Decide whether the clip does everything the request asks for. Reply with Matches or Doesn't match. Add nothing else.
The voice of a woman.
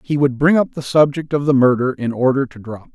Doesn't match